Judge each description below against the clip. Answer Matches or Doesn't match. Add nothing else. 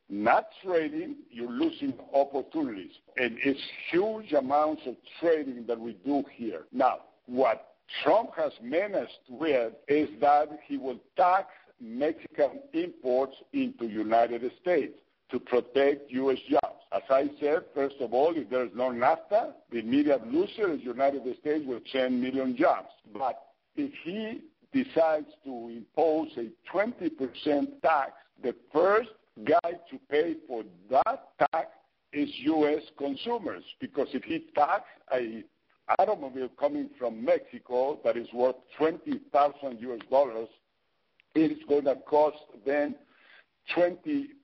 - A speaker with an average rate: Doesn't match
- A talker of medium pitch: Matches